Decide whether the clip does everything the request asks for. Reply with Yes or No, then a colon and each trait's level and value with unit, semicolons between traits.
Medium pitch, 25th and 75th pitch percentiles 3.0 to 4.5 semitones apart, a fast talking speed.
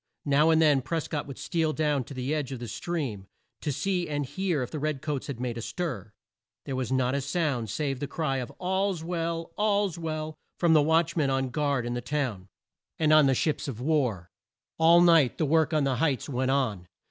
Yes: medium, 145 Hz; average, 3.9 semitones; fast, 220 wpm